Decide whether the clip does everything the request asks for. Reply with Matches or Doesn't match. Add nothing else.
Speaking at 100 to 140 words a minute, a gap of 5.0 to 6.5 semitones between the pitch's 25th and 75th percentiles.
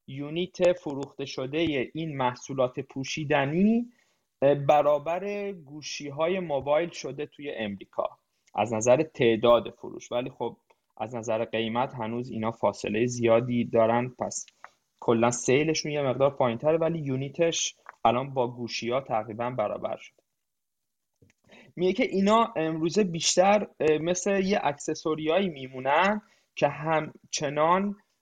Matches